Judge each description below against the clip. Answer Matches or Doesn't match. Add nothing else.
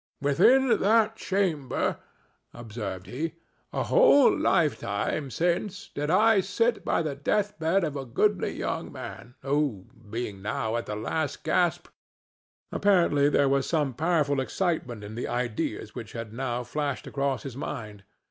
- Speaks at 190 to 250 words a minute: Doesn't match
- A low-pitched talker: Doesn't match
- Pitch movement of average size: Doesn't match